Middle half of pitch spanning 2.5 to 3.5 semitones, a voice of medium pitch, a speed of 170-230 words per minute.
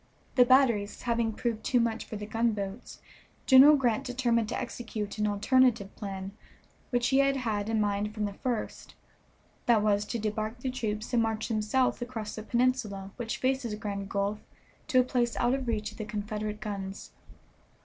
No: average, 2.8 semitones; high, 225 Hz; average, 180 wpm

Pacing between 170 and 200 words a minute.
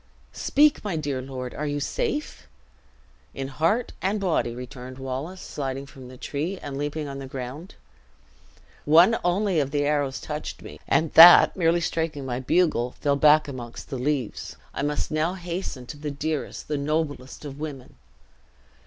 No: average, 160 wpm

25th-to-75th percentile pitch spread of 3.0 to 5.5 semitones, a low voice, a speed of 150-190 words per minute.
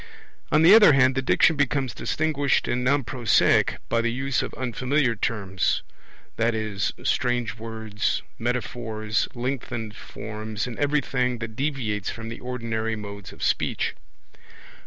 No: average, 3.3 semitones; low, 120 Hz; slow, 135 wpm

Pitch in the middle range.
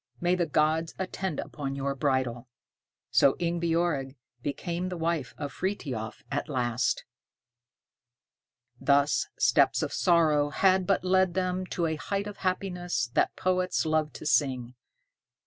Yes: medium, 160 Hz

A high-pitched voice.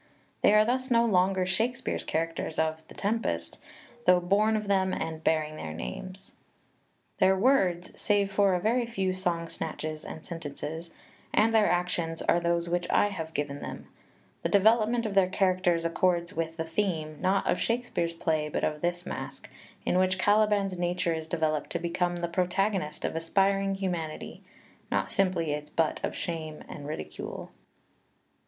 No: medium, 180 Hz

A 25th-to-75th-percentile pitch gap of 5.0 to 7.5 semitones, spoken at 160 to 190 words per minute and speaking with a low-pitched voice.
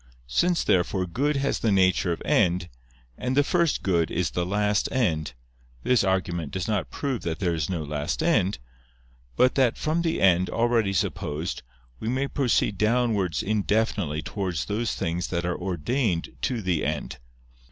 Yes: wide, 5.6 semitones; average, 165 wpm; very low, 95 Hz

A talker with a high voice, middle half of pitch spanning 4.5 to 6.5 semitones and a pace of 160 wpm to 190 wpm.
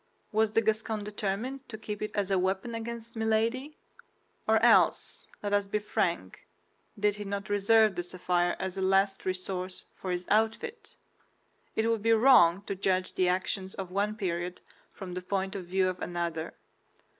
No: high, 200 Hz; average, 3.0 semitones; average, 170 wpm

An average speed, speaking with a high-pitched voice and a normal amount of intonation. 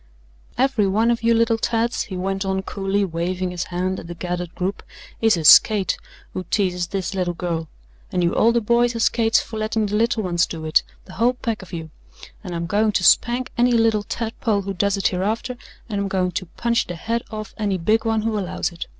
No: fast, 220 wpm; high, 200 Hz; average, 3.8 semitones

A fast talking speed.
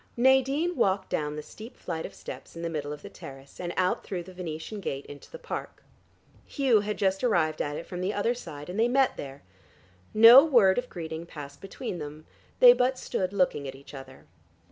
Yes: fast, 210 wpm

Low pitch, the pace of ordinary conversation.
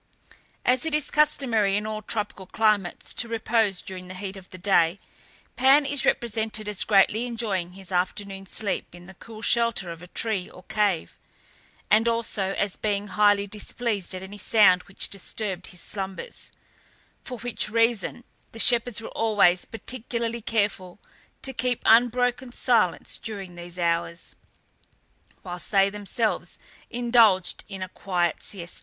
No: high, 210 Hz; average, 150 wpm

